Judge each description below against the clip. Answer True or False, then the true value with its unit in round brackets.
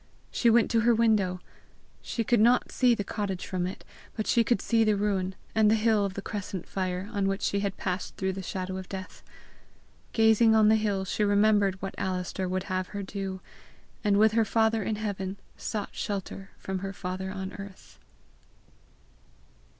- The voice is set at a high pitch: True (200 Hz)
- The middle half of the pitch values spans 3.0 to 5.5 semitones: False (2.4 semitones)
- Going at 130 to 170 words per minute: False (185 wpm)